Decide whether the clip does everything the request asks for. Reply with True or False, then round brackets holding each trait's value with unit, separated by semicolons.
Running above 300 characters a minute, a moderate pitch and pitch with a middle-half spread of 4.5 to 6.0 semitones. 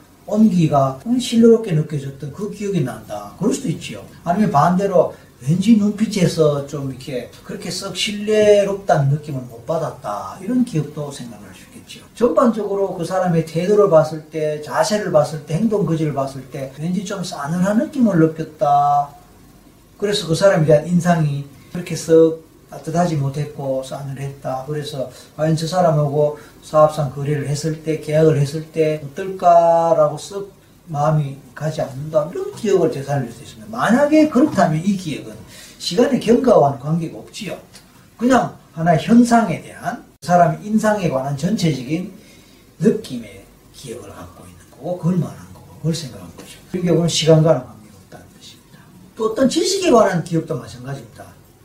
True (345 characters per minute; 160 Hz; 5.5 semitones)